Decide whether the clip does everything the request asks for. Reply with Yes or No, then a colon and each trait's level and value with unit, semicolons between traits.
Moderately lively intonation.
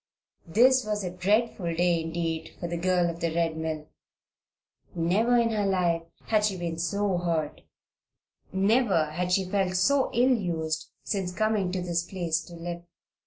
Yes: average, 3.5 semitones